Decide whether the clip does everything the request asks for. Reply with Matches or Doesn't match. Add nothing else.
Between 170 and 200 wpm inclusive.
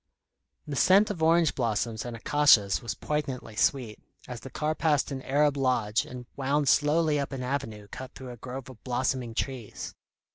Matches